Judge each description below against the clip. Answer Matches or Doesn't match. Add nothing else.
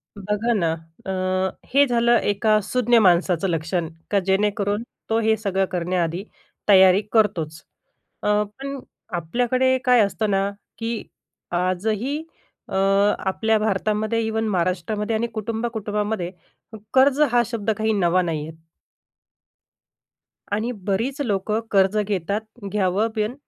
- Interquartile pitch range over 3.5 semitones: Doesn't match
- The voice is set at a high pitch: Matches